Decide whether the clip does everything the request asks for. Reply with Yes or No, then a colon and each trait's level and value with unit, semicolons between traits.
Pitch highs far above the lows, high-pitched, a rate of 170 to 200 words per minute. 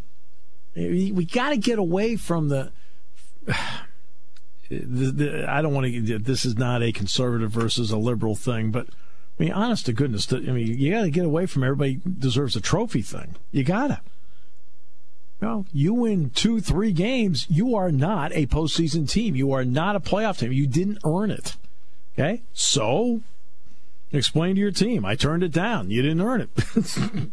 No: wide, 8.3 semitones; medium, 140 Hz; average, 180 wpm